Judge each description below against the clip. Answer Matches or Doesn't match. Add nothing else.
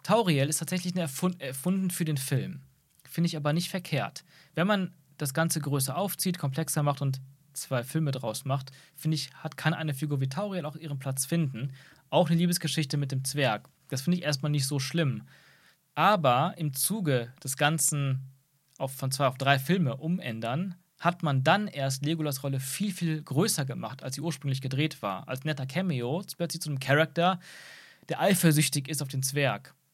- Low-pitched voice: Doesn't match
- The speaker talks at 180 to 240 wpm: Matches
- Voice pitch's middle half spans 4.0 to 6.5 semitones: Doesn't match